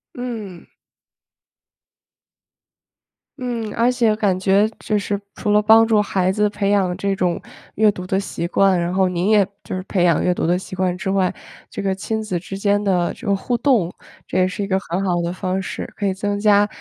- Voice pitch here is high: Yes, high, 195 Hz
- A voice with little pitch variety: Yes, narrow, 2.3 semitones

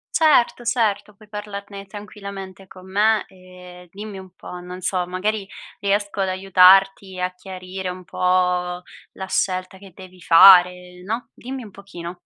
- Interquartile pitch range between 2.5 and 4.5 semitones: No, narrow, 1.9 semitones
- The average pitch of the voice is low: No, high, 190 Hz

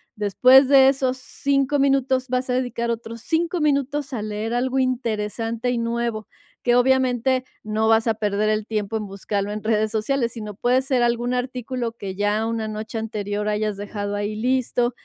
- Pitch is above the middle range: Yes, high, 235 Hz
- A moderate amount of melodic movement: Yes, average, 3.2 semitones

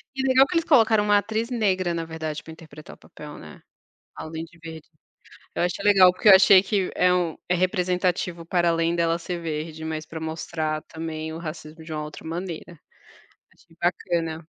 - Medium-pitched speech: Yes, medium, 170 Hz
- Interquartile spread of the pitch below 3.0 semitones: Yes, narrow, 2.6 semitones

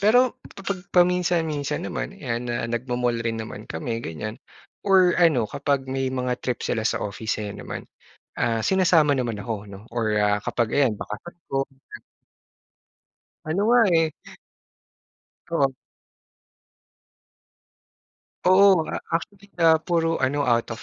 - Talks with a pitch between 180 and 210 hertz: No, low, 135 Hz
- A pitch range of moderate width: No, wide, 7.0 semitones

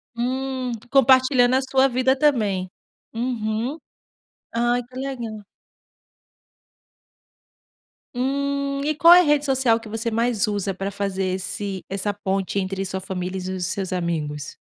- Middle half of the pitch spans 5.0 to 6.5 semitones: Yes, average, 5.3 semitones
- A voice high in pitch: Yes, high, 230 Hz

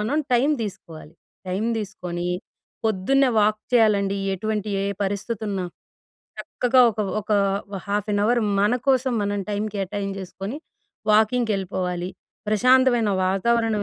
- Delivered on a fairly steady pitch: No, average, 3.1 semitones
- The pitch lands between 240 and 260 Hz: No, high, 210 Hz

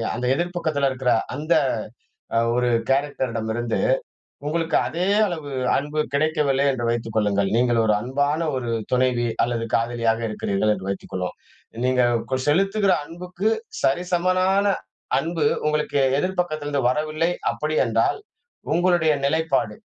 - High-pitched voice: No, medium, 145 Hz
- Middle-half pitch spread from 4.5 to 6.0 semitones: Yes, wide, 5.5 semitones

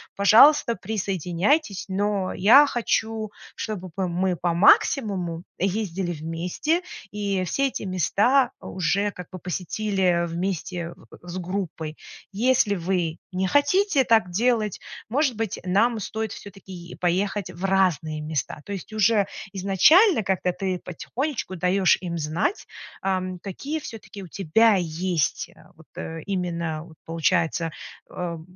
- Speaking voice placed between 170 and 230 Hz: Yes, high, 190 Hz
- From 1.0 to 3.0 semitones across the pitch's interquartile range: No, average, 3.7 semitones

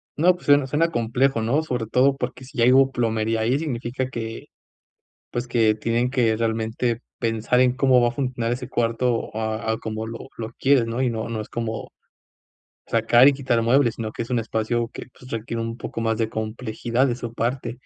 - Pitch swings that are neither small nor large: No, narrow, 2.2 semitones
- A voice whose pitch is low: Yes, low, 120 Hz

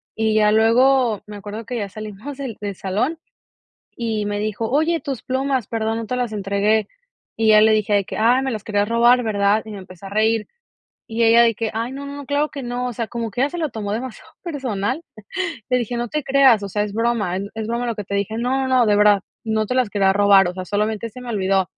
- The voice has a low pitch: No, high, 220 Hz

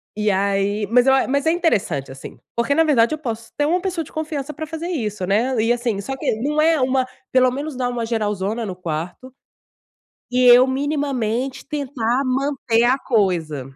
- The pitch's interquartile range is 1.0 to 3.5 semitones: No, average, 5.1 semitones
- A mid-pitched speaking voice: No, very high, 250 Hz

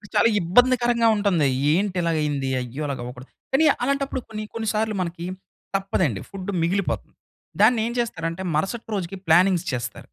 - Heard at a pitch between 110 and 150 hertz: No, high, 190 Hz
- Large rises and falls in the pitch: Yes, wide, 5.7 semitones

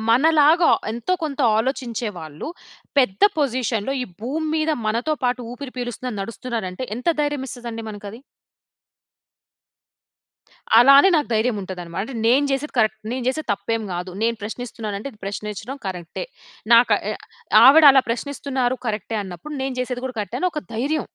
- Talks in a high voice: Yes, high, 245 Hz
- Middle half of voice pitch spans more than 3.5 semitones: Yes, average, 4.0 semitones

